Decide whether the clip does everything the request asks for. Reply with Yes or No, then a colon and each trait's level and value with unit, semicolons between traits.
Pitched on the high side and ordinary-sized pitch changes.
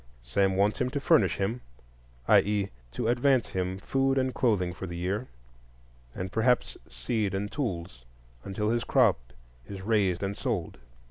No: low, 100 Hz; average, 4.6 semitones